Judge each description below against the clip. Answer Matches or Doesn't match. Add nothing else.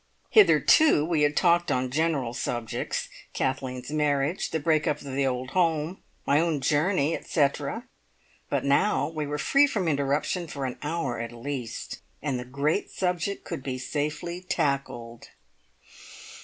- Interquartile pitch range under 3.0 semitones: Doesn't match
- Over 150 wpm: Doesn't match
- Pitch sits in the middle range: Matches